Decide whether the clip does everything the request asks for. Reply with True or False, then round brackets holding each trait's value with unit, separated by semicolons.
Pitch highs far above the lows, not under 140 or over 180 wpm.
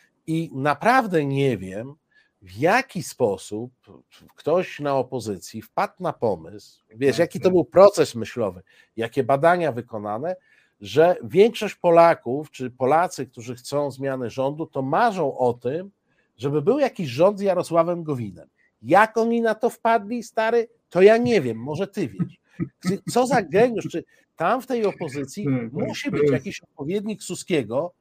True (7.3 semitones; 145 wpm)